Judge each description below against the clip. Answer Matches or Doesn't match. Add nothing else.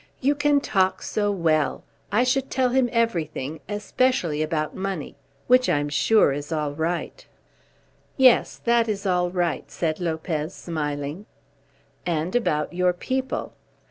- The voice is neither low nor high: Matches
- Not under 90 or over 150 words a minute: Matches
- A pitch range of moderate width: Doesn't match